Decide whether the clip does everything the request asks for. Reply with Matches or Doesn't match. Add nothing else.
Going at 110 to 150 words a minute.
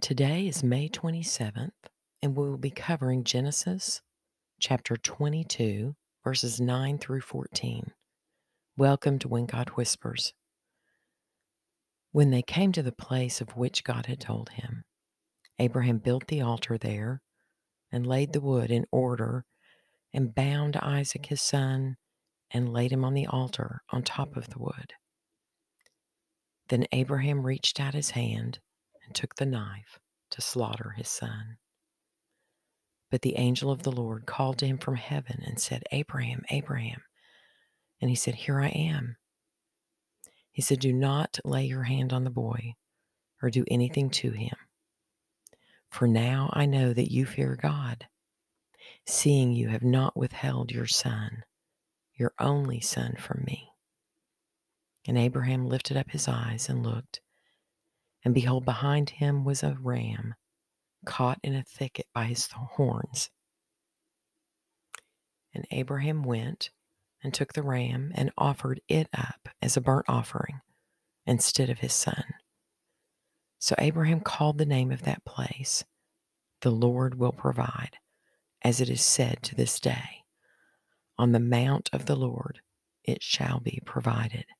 Matches